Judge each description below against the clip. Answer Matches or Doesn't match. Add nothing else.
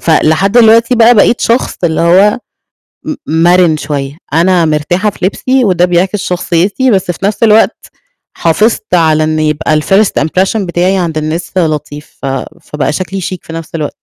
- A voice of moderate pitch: Matches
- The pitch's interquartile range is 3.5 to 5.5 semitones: Matches